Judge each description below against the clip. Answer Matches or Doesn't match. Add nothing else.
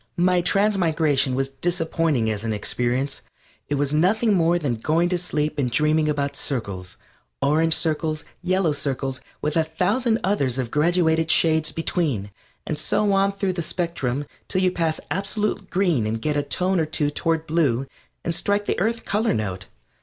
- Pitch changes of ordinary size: Matches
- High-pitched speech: Doesn't match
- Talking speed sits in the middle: Matches